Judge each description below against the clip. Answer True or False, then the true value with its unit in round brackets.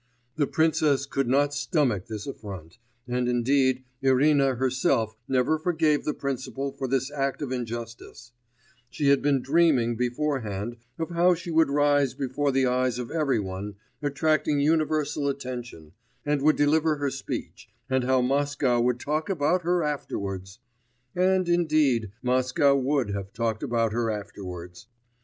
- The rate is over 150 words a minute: False (145 wpm)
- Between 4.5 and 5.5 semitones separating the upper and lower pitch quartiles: False (3.7 semitones)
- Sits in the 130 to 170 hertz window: True (135 Hz)